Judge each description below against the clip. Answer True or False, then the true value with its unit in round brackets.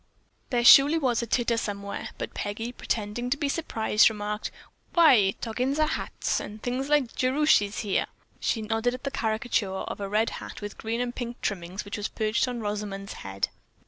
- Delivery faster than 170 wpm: True (180 wpm)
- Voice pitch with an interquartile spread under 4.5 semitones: True (3.3 semitones)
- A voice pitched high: True (225 Hz)